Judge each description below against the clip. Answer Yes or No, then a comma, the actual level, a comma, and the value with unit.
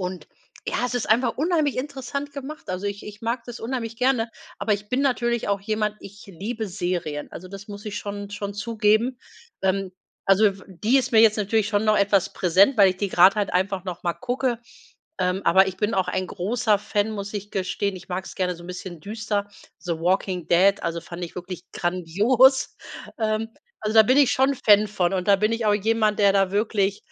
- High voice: Yes, high, 205 Hz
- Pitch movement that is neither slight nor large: Yes, average, 3.2 semitones